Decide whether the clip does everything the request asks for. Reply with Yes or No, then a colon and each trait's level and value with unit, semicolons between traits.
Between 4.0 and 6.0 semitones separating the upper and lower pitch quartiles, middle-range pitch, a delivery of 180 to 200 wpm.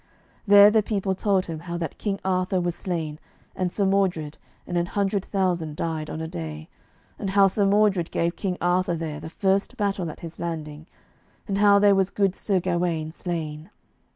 No: average, 3.3 semitones; medium, 180 Hz; average, 185 wpm